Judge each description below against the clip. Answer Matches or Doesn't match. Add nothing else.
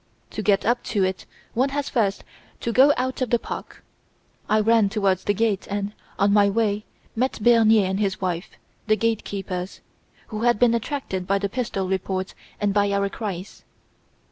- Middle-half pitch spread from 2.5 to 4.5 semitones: Matches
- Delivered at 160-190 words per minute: Matches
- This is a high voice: Matches